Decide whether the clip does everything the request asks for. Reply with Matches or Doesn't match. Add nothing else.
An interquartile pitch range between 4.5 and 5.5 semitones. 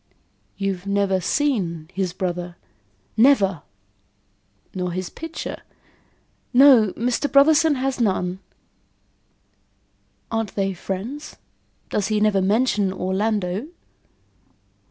Matches